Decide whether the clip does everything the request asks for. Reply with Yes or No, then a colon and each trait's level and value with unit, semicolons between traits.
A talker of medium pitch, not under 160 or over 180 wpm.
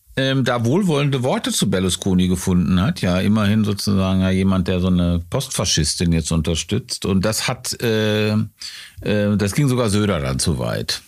No: low, 100 Hz; average, 170 wpm